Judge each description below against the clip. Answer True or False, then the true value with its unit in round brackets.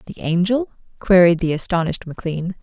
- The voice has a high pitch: False (180 Hz)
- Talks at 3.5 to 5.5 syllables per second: False (6.3 syllables/s)